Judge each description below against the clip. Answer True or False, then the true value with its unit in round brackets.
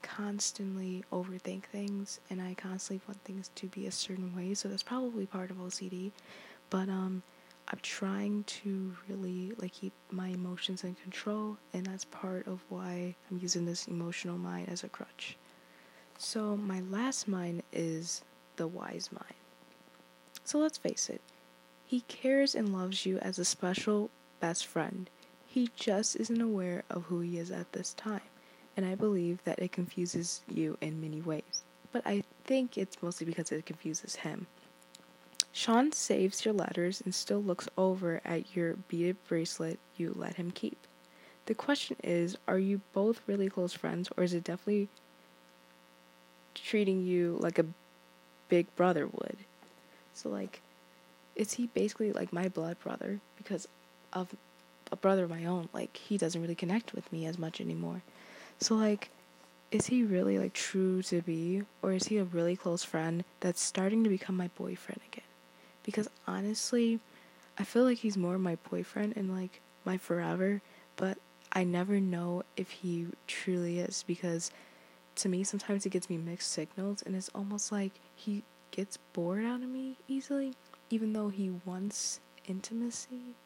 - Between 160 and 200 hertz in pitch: True (185 Hz)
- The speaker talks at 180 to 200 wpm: False (165 wpm)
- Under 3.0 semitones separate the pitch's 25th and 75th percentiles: False (3.5 semitones)